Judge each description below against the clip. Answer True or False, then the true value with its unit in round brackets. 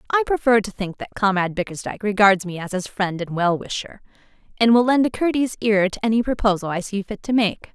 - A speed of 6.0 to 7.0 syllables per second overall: True (6.3 syllables/s)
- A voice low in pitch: False (210 Hz)